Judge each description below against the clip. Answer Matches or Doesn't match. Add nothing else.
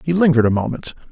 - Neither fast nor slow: Doesn't match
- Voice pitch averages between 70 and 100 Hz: Doesn't match